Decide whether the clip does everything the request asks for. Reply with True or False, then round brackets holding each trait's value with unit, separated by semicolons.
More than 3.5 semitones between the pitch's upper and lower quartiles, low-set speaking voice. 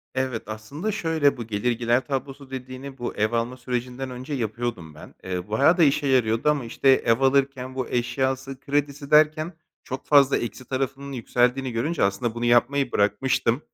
False (2.8 semitones; 130 Hz)